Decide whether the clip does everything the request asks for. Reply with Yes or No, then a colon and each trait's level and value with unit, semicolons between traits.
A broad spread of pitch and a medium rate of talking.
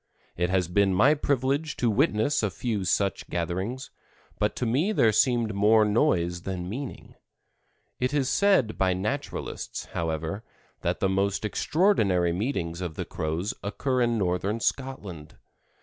Yes: wide, 5.8 semitones; average, 145 wpm